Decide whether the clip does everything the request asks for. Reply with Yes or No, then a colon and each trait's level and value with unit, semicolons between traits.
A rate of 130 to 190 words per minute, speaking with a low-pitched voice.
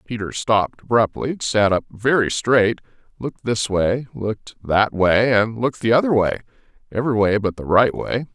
Yes: average, 175 wpm; low, 110 Hz